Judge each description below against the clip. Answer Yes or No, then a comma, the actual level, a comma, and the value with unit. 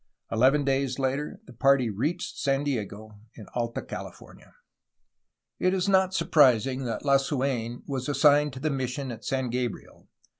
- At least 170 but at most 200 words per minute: No, average, 150 wpm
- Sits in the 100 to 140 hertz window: Yes, low, 135 Hz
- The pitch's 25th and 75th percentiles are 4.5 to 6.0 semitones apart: No, average, 2.9 semitones